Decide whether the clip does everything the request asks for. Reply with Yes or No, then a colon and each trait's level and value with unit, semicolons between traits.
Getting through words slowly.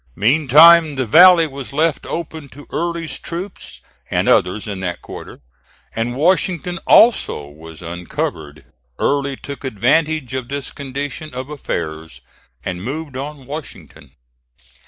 Yes: slow, 125 wpm